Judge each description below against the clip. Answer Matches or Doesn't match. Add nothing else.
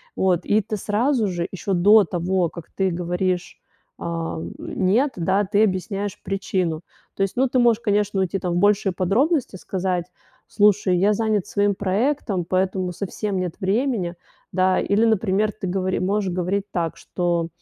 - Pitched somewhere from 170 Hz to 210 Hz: Matches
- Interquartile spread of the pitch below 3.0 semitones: Matches